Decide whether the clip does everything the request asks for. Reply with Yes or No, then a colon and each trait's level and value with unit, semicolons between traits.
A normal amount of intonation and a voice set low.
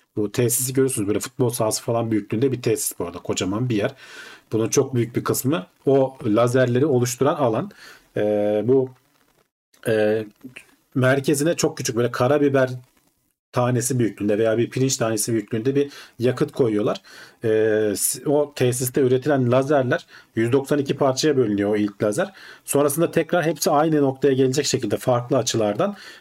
Yes: average, 4.0 semitones; low, 130 Hz